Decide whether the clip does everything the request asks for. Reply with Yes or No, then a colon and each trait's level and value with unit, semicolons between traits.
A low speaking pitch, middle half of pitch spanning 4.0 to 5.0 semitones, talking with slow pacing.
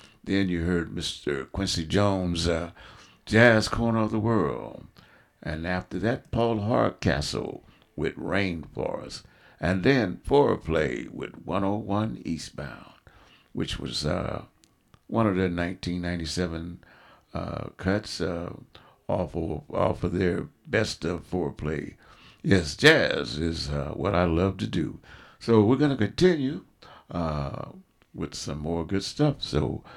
Yes: very low, 95 Hz; average, 4.5 semitones; slow, 130 wpm